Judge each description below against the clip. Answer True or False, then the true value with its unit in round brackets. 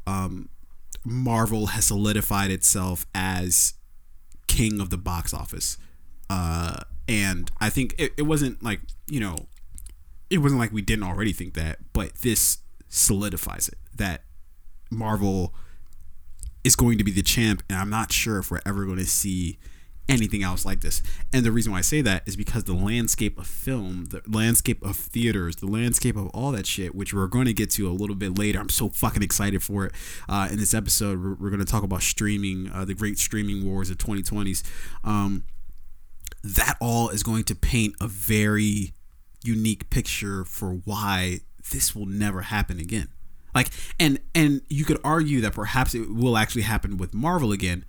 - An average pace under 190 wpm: True (180 wpm)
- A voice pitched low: True (100 Hz)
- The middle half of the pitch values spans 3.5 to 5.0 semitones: True (3.8 semitones)